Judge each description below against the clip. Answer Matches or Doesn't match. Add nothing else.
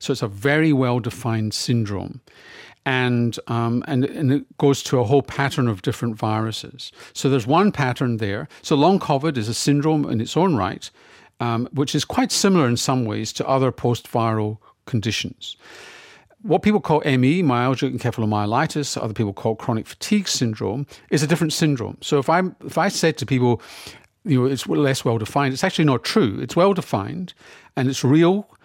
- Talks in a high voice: Doesn't match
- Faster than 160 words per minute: Matches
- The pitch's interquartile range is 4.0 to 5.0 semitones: Matches